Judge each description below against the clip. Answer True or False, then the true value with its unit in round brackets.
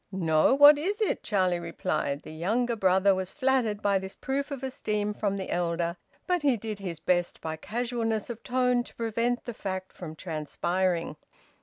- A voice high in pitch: True (205 Hz)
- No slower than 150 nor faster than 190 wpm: True (175 wpm)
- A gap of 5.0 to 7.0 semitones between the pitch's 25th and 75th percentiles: True (5.6 semitones)